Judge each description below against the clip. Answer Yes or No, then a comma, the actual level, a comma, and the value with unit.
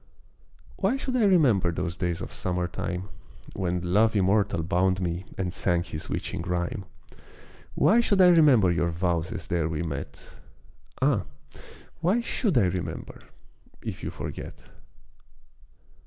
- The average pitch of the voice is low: Yes, very low, 95 Hz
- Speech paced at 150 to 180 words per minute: No, average, 140 wpm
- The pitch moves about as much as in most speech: No, wide, 6.3 semitones